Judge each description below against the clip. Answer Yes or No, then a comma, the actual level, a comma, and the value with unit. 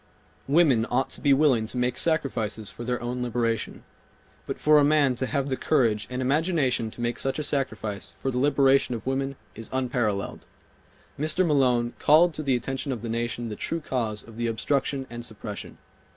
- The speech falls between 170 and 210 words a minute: Yes, average, 190 wpm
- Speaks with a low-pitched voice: Yes, low, 125 Hz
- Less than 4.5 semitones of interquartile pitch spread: Yes, average, 3.2 semitones